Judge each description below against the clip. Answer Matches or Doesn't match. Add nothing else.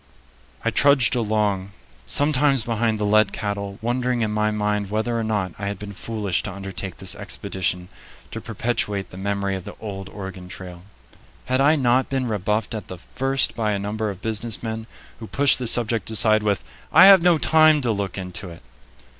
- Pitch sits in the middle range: Doesn't match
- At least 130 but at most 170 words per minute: Doesn't match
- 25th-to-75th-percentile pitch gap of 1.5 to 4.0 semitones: Matches